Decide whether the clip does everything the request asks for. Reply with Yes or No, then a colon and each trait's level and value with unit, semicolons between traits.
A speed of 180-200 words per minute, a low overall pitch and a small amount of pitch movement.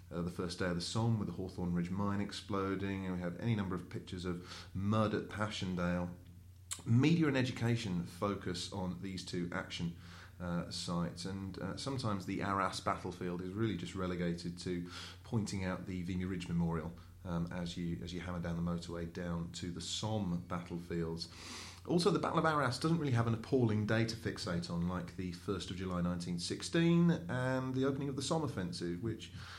No: average, 190 wpm; very low, 90 Hz; average, 3.2 semitones